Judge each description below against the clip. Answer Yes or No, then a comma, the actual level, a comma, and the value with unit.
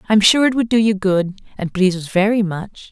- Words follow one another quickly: Yes, fast, 245 wpm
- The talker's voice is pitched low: No, high, 200 Hz